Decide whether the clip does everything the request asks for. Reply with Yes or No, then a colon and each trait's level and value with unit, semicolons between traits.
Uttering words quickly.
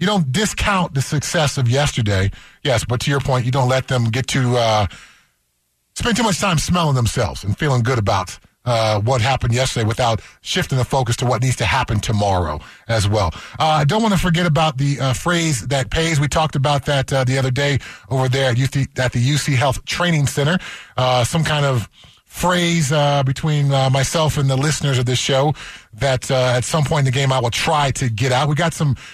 Yes: fast, 220 wpm